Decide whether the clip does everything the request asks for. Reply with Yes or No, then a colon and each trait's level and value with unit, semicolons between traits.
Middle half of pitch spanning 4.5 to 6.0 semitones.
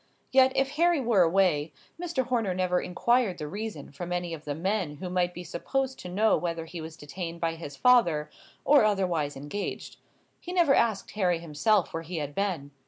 Yes: average, 5.2 semitones